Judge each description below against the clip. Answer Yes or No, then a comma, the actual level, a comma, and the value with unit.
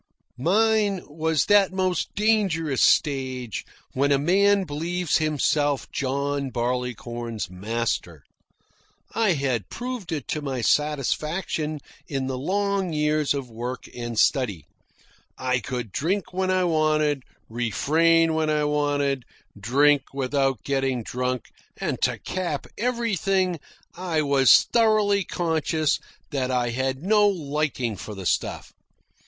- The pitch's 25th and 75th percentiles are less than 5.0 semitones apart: No, wide, 5.6 semitones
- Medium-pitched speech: Yes, medium, 145 Hz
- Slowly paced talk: Yes, slow, 120 wpm